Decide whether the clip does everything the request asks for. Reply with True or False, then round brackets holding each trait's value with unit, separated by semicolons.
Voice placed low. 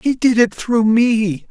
False (225 Hz)